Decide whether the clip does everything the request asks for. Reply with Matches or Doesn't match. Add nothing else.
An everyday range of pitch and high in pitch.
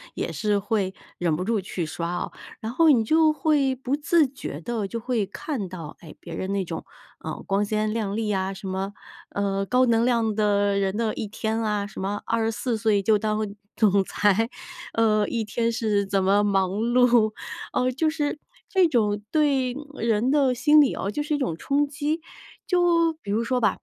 Matches